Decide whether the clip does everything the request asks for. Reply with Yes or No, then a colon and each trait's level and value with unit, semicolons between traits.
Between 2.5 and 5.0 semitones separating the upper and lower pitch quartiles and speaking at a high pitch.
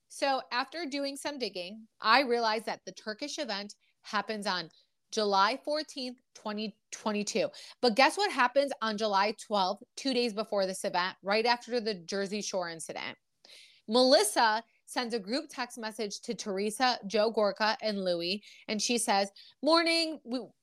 Yes: average, 4.0 semitones; high, 220 Hz